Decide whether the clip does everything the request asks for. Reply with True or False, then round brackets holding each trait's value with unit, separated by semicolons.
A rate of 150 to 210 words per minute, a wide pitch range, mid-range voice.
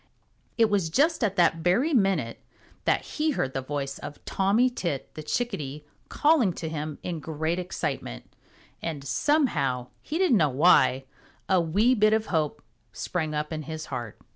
True (165 wpm; 6.5 semitones; 165 Hz)